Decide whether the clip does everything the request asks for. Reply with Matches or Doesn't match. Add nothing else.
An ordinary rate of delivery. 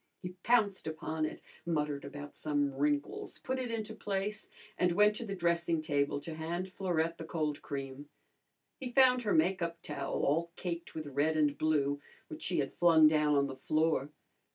Matches